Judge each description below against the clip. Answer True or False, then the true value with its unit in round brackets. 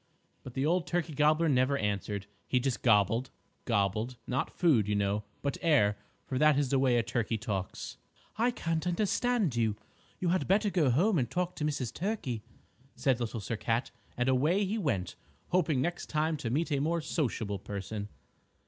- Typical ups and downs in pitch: False (6.6 semitones)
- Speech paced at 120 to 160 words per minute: False (180 wpm)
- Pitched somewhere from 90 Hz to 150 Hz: True (135 Hz)